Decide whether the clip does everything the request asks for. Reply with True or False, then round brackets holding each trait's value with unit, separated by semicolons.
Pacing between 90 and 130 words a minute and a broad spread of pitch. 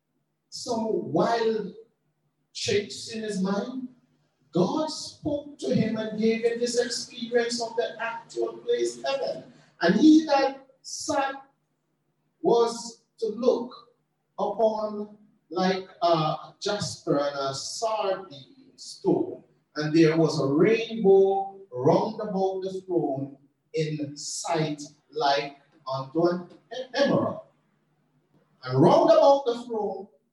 True (110 wpm; 6.8 semitones)